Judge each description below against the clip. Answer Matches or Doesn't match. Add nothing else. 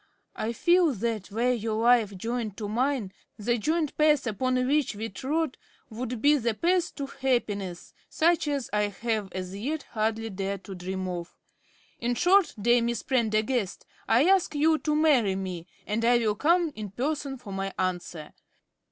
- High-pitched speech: Matches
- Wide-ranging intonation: Matches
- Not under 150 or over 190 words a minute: Matches